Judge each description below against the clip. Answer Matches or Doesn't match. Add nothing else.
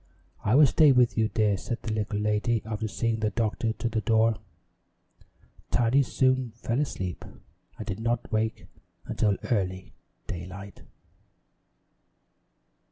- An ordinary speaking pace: Doesn't match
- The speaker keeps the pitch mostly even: Matches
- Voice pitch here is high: Doesn't match